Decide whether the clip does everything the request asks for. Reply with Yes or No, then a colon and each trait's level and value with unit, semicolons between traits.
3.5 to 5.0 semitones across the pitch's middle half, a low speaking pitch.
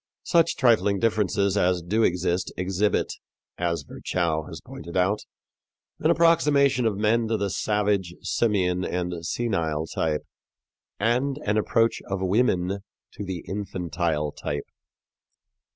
Yes: average, 4.1 semitones; low, 100 Hz